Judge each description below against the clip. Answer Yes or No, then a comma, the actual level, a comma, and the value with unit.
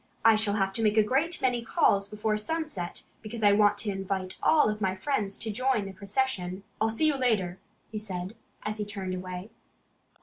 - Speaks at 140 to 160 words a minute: No, average, 195 wpm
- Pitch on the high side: Yes, high, 210 Hz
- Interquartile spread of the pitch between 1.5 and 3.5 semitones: Yes, average, 2.8 semitones